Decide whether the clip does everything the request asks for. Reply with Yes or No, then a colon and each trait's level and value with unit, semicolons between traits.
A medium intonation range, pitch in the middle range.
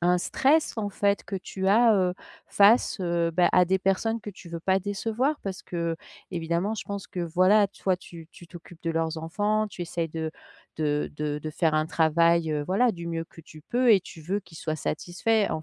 Yes: average, 3.7 semitones; medium, 180 Hz